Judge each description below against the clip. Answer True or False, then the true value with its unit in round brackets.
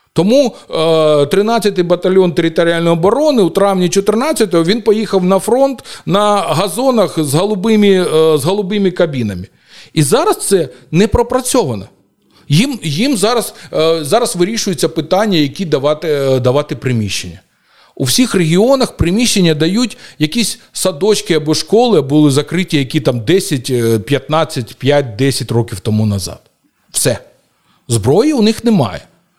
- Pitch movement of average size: False (6.2 semitones)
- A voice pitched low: False (170 Hz)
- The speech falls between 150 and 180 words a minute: False (120 wpm)